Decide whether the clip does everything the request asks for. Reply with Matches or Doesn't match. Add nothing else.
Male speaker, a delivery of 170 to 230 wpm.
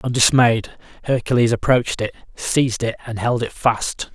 Doesn't match